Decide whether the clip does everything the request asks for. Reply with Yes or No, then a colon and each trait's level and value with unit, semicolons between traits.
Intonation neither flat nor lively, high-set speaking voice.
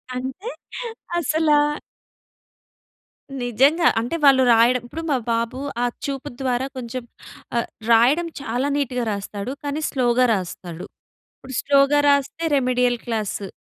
Yes: average, 3.1 semitones; very high, 255 Hz